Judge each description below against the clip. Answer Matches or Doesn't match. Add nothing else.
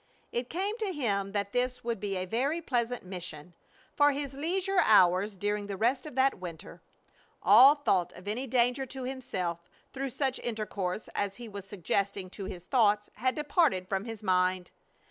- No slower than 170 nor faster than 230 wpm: Matches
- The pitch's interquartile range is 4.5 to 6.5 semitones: Matches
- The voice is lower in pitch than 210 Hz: Doesn't match